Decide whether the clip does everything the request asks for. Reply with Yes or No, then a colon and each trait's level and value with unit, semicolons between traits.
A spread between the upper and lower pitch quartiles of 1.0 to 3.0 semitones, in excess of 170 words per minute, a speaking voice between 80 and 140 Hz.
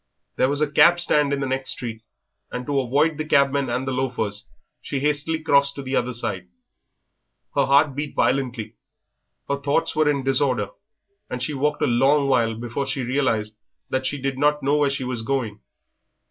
Yes: narrow, 2.5 semitones; average, 190 wpm; low, 135 Hz